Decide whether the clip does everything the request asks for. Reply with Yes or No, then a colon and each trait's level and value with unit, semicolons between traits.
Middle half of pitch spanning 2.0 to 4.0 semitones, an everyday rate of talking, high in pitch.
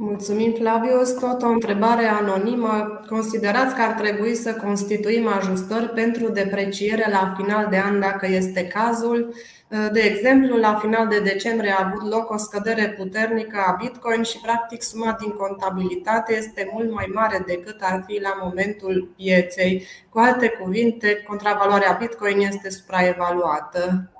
Yes: average, 2.7 semitones; average, 145 wpm; high, 210 Hz